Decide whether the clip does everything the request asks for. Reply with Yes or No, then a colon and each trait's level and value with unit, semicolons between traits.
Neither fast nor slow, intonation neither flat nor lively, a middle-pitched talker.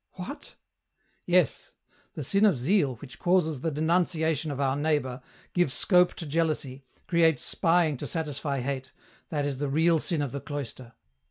Yes: average, 165 wpm; average, 3.4 semitones; medium, 155 Hz